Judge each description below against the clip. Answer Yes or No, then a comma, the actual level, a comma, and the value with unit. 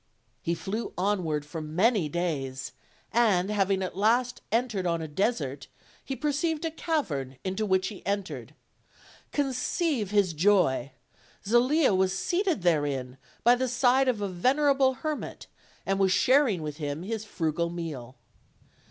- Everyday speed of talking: Yes, average, 145 wpm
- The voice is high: Yes, high, 195 Hz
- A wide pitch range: Yes, wide, 7.2 semitones